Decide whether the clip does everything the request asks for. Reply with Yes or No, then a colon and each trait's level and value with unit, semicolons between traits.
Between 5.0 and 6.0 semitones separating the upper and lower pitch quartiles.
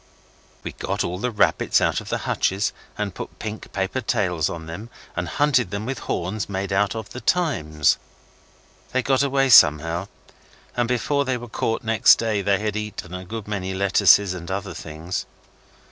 No: average, 4.3 semitones